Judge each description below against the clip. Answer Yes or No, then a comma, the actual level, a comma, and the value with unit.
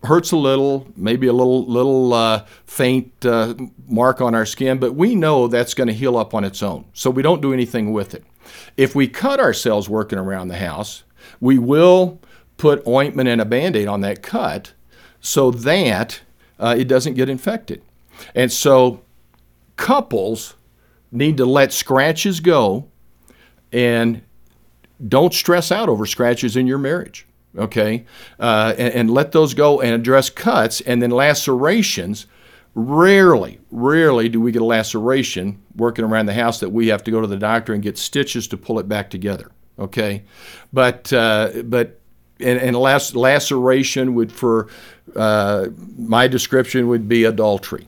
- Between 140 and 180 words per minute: Yes, average, 165 wpm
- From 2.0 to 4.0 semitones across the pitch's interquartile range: Yes, average, 3.7 semitones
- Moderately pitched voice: No, low, 120 Hz